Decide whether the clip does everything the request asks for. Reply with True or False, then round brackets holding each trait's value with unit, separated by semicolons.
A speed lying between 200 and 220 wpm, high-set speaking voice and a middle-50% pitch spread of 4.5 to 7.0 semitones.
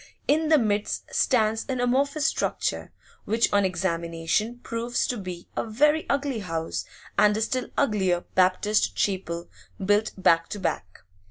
False (145 wpm; 210 Hz; 5.2 semitones)